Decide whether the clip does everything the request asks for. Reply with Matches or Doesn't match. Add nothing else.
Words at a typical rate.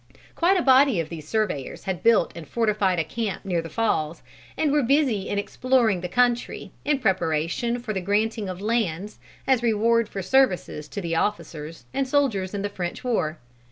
Matches